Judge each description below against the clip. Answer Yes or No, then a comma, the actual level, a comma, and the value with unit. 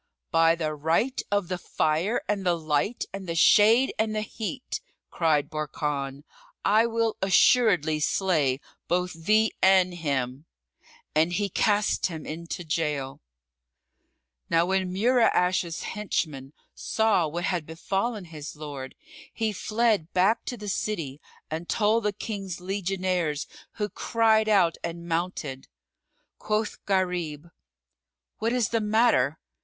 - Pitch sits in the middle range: Yes, medium, 180 Hz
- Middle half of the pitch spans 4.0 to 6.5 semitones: Yes, average, 5.0 semitones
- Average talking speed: No, slow, 130 wpm